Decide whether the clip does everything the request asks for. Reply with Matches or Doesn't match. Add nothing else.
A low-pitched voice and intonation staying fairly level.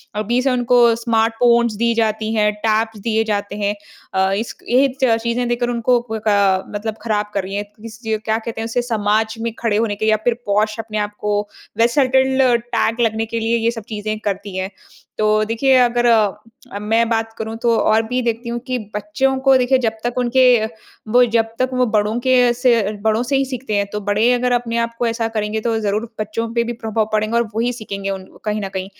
Doesn't match